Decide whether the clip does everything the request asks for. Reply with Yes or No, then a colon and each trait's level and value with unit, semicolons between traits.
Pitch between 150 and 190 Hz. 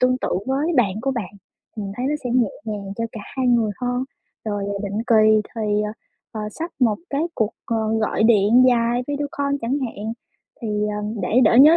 No: high, 230 Hz